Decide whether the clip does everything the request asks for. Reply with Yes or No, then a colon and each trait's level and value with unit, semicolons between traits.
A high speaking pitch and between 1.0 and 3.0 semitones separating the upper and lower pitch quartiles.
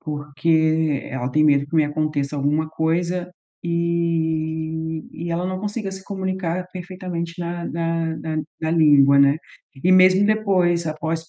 No: medium, 165 Hz; narrow, 2.5 semitones